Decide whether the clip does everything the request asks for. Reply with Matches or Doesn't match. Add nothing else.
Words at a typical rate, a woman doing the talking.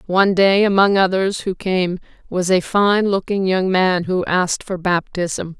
Matches